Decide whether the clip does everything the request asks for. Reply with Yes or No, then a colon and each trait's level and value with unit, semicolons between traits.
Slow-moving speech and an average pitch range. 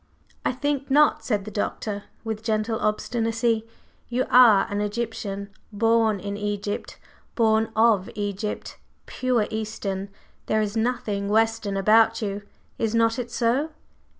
No: slow, 130 wpm; narrow, 2.0 semitones